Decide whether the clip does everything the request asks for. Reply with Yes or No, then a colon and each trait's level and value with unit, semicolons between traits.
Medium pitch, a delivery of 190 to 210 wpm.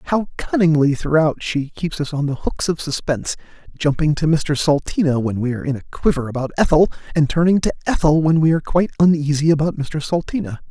Yes: medium, 155 Hz; average, 195 wpm